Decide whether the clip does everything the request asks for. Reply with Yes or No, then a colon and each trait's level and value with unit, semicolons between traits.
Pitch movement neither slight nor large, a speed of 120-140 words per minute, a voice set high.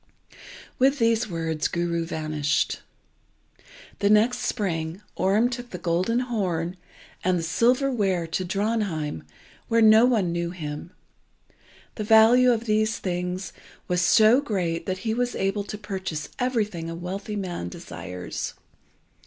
Yes: average, 4.8 semitones; slow, 135 wpm; high, 195 Hz